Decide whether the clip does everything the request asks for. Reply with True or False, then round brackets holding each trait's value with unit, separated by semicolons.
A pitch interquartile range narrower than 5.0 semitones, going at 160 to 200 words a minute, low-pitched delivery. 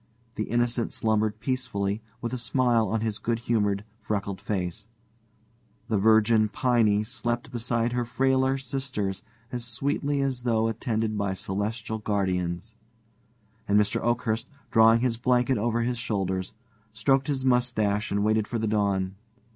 False (2.8 semitones; 140 wpm; 110 Hz)